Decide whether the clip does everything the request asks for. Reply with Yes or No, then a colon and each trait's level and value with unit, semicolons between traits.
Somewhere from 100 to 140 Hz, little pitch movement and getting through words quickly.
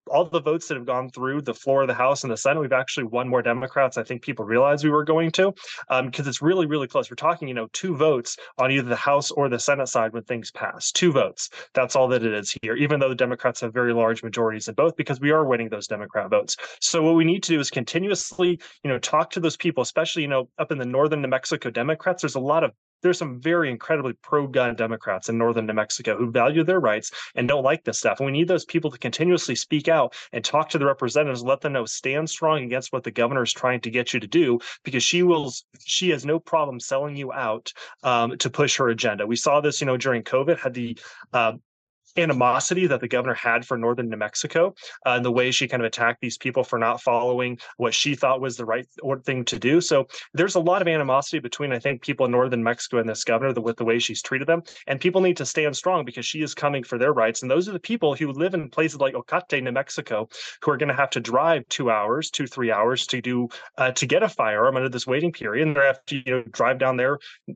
No: low, 135 Hz; average, 4.3 semitones; fast, 260 wpm